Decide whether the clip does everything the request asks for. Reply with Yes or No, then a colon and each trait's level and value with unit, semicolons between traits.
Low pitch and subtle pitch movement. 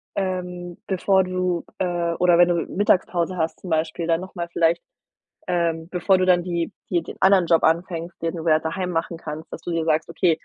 No: medium, 175 Hz; narrow, 1.7 semitones